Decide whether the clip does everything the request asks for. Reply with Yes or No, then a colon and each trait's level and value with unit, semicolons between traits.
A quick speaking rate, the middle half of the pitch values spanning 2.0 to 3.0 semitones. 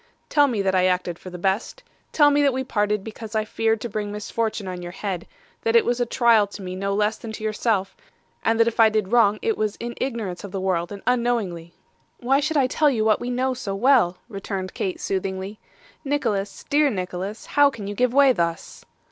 No: fast, 225 wpm; average, 4.2 semitones